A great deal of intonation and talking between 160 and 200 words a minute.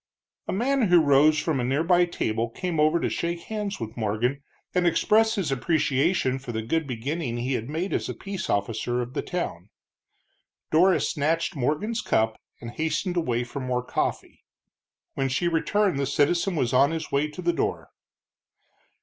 Yes: wide, 5.8 semitones; average, 175 wpm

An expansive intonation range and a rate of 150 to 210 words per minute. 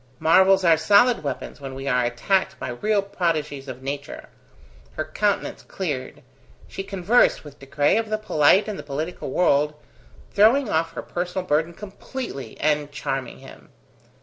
Yes: wide, 5.7 semitones; average, 155 wpm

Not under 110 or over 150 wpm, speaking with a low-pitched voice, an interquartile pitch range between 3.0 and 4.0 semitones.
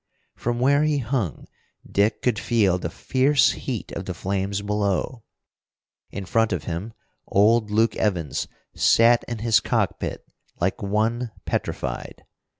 Yes: slow, 135 wpm; low, 110 Hz; average, 3.4 semitones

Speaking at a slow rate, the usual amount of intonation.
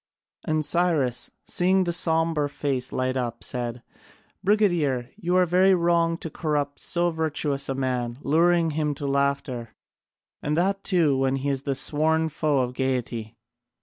No: average, 150 wpm; average, 4.4 semitones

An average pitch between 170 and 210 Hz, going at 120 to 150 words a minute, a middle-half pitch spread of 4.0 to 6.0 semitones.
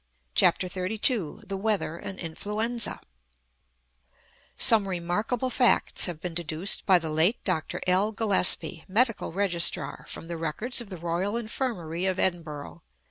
Yes: medium, 185 Hz; slow, 135 wpm; average, 4.3 semitones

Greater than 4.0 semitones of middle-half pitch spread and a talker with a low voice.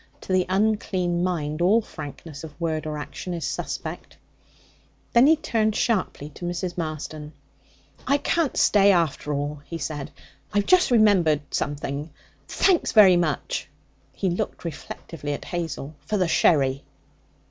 No: average, 5.0 semitones; medium, 170 Hz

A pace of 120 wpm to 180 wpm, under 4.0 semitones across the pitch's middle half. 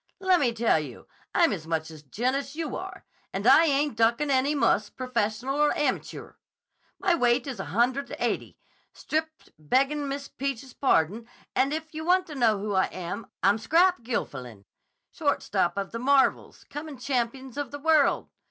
No: average, 170 wpm; average, 5.3 semitones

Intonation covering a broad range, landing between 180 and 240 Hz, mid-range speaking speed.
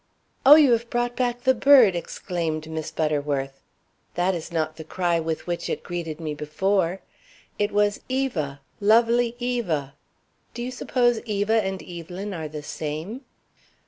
Yes: wide, 7.0 semitones; medium, 185 Hz; average, 150 wpm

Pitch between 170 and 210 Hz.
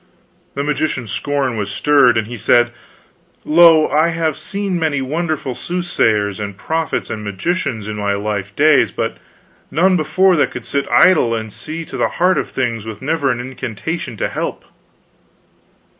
No: medium, 140 Hz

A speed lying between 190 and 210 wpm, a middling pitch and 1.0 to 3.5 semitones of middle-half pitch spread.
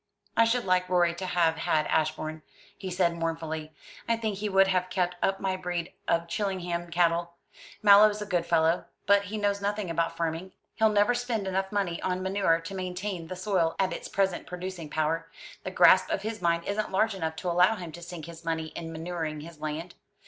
Yes: average, 200 wpm; medium, 180 Hz; average, 2.9 semitones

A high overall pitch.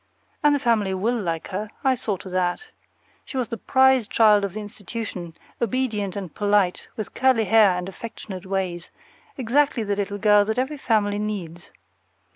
Yes: high, 210 Hz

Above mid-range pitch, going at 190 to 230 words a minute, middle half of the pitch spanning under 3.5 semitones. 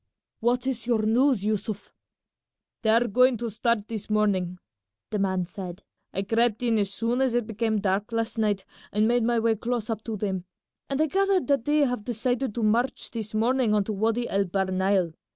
Yes: high, 220 Hz; average, 200 wpm; average, 2.9 semitones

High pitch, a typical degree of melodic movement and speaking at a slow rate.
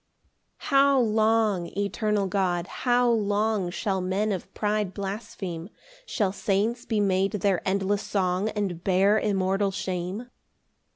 No: high, 200 Hz; narrow, 2.3 semitones; slow, 130 wpm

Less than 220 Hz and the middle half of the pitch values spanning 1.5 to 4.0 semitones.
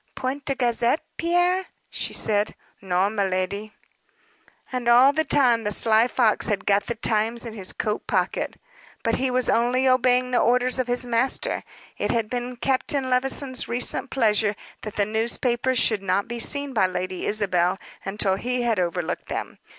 No: high, 235 Hz; average, 3.5 semitones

